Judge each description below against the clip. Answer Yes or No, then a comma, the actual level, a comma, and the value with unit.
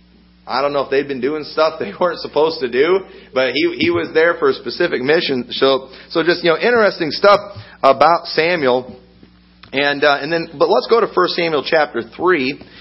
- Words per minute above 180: Yes, average, 200 wpm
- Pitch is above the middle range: No, medium, 160 Hz